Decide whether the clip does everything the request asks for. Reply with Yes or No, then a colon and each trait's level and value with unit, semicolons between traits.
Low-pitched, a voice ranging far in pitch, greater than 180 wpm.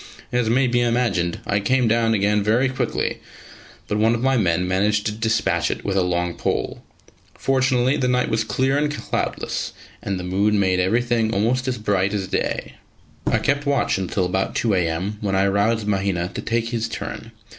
No: low, 105 Hz; average, 3.9 semitones; average, 190 wpm